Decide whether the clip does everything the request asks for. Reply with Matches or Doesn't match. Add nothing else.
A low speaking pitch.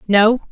Doesn't match